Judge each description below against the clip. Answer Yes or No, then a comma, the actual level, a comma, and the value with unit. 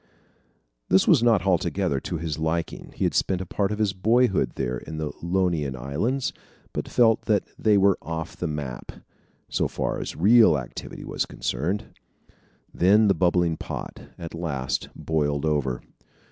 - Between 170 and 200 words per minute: No, average, 160 wpm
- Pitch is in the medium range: No, very low, 85 Hz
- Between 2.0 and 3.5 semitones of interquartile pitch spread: No, average, 5.1 semitones